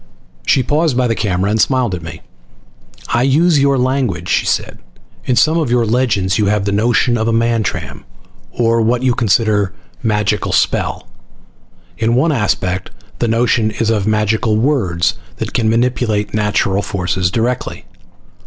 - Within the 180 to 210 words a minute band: No, average, 155 wpm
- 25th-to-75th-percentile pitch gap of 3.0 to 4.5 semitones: Yes, average, 3.3 semitones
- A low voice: Yes, low, 115 Hz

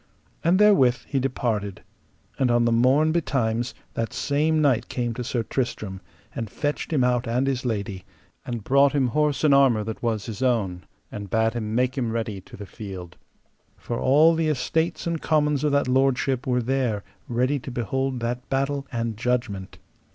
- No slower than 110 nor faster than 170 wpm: No, average, 180 wpm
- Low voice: Yes, low, 125 Hz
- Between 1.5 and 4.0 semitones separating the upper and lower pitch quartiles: Yes, average, 3.4 semitones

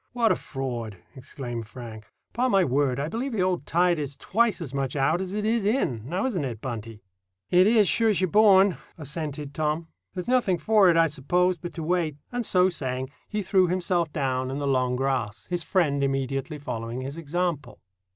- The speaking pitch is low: No, medium, 155 Hz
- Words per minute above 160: Yes, average, 195 wpm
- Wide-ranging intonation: Yes, wide, 5.8 semitones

